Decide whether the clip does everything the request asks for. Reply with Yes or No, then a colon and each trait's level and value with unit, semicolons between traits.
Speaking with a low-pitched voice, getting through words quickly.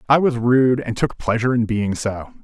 Yes: low, 120 Hz; fast, 220 wpm